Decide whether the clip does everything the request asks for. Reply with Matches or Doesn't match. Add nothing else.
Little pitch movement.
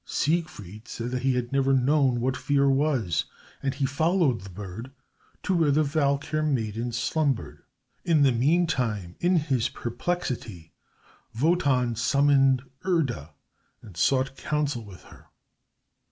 Doesn't match